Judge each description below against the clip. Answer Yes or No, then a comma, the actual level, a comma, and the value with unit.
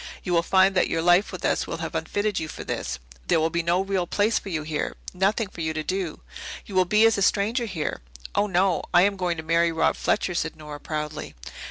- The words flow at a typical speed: No, fast, 240 wpm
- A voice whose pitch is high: No, medium, 180 Hz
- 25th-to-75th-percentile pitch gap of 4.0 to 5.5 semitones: No, average, 3.4 semitones